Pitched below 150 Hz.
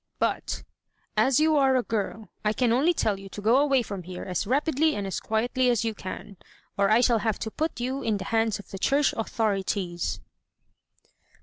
No: high, 225 Hz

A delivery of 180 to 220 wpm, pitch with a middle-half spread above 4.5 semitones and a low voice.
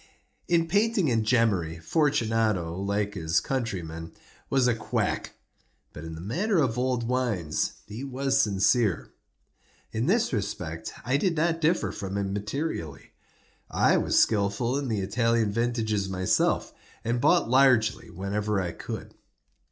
No: slow, 135 wpm; average, 5.1 semitones; low, 110 Hz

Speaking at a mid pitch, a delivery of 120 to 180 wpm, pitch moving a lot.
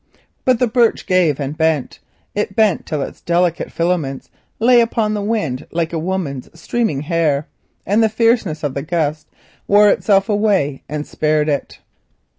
Yes: medium, 170 Hz; average, 160 wpm; wide, 5.9 semitones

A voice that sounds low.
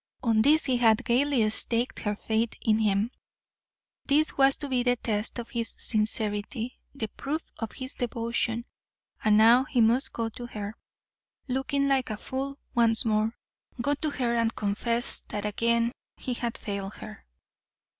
No: high, 235 Hz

